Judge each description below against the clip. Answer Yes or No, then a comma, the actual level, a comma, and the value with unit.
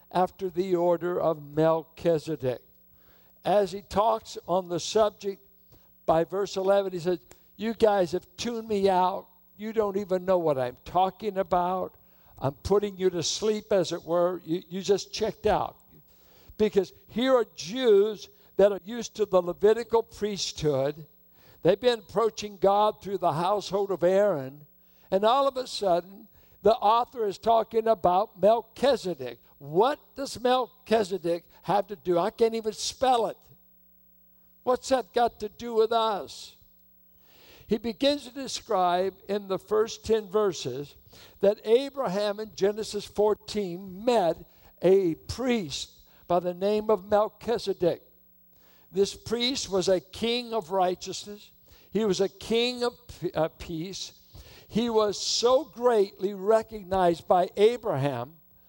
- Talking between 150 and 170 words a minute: No, slow, 135 wpm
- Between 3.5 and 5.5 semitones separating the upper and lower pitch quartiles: Yes, average, 3.9 semitones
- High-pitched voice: Yes, high, 200 Hz